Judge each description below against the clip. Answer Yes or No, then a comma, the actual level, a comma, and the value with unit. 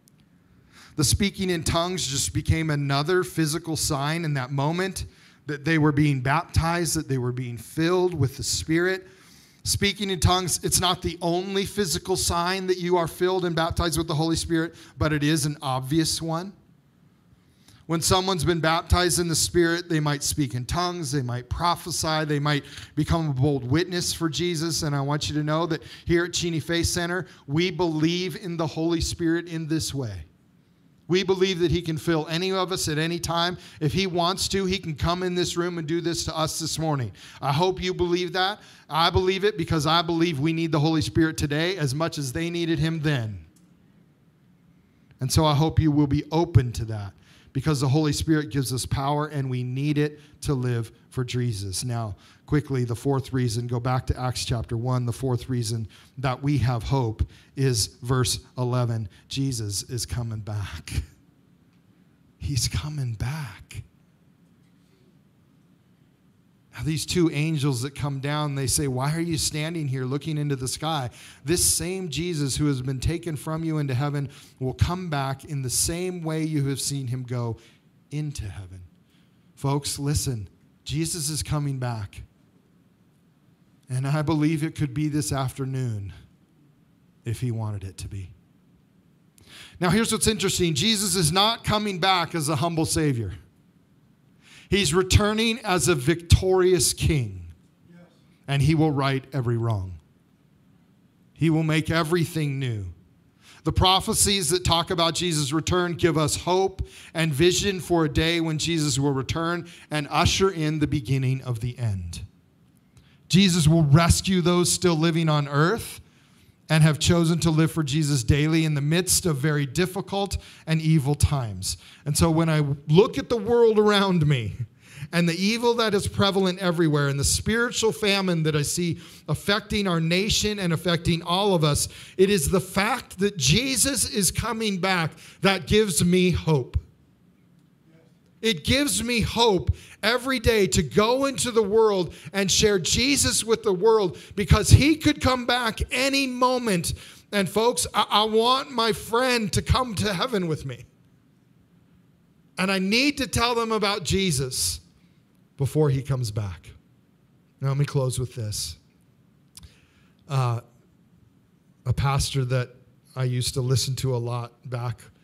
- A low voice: No, medium, 155 Hz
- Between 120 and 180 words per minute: Yes, average, 165 wpm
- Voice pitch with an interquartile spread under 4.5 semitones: No, average, 4.8 semitones